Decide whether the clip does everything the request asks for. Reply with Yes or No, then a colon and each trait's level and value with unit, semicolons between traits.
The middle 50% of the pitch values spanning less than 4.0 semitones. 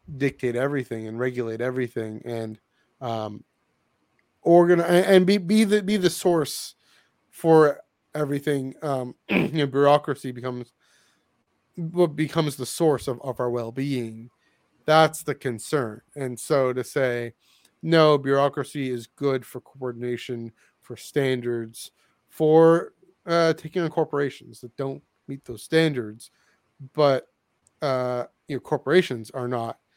No: average, 4.3 semitones